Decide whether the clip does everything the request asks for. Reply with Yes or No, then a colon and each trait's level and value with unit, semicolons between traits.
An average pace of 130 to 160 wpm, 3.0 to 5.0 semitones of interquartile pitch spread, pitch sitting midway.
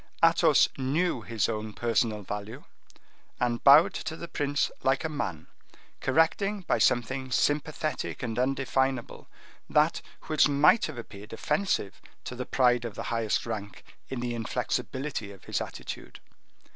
No: average, 140 wpm; average, 4.5 semitones; low, 125 Hz